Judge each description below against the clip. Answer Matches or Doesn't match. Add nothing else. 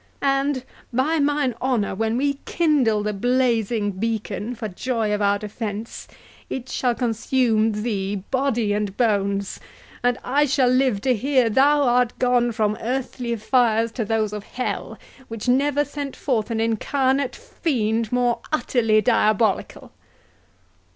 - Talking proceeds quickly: Doesn't match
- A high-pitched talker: Matches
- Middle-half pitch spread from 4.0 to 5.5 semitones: Doesn't match